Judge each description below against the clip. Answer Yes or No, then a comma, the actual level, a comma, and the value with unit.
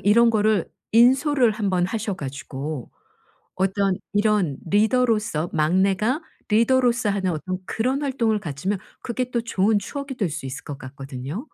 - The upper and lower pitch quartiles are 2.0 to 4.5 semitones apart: No, average, 5.3 semitones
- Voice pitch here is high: Yes, high, 205 Hz